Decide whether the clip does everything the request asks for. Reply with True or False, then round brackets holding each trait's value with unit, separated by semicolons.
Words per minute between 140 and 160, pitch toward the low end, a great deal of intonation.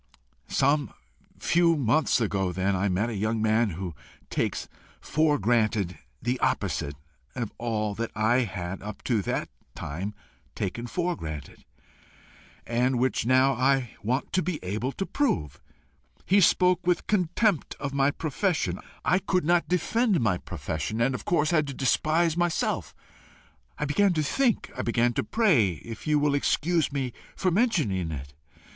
True (155 wpm; 130 Hz; 7.8 semitones)